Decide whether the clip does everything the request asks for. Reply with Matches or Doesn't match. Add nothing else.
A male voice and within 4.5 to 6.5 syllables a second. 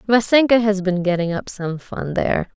Doesn't match